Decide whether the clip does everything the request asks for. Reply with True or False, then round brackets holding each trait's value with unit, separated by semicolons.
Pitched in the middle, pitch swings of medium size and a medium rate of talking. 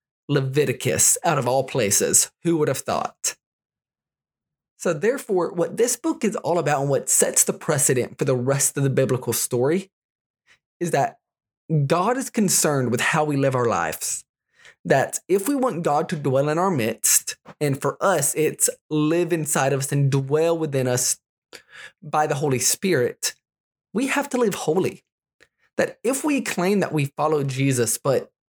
False (155 Hz; 6.0 semitones; 170 wpm)